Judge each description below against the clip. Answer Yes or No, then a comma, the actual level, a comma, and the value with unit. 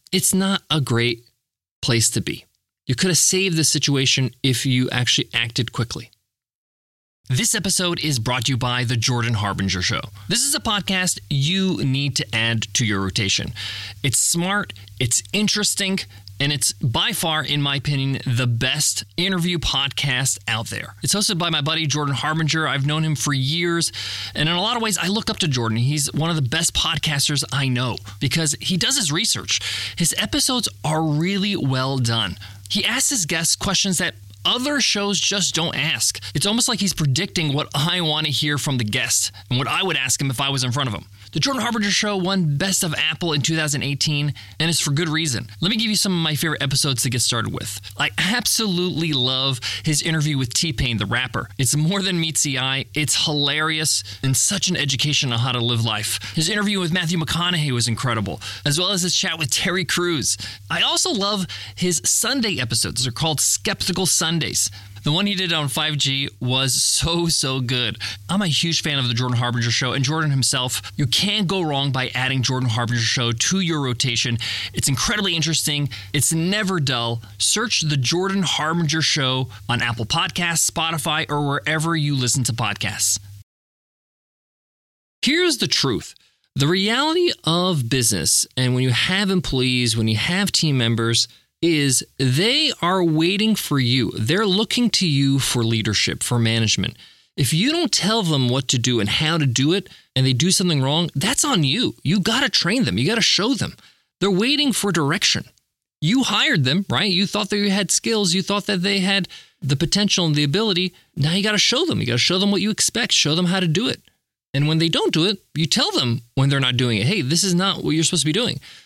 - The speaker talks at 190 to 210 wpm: Yes, average, 200 wpm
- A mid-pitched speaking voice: Yes, medium, 145 Hz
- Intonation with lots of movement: Yes, wide, 6.5 semitones